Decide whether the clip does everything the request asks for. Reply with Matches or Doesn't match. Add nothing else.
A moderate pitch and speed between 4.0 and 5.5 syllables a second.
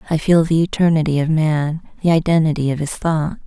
Doesn't match